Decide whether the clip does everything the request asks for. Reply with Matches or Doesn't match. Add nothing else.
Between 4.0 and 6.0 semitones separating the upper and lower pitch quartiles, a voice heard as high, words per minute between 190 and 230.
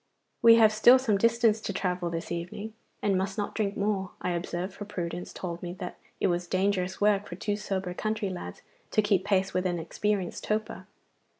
Doesn't match